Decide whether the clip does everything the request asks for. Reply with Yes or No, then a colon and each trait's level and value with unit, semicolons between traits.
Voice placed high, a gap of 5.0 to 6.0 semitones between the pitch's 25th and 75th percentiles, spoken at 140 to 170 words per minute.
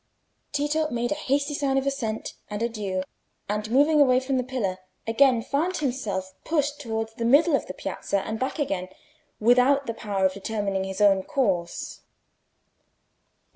Yes: high, 240 Hz; average, 5.3 semitones; average, 160 wpm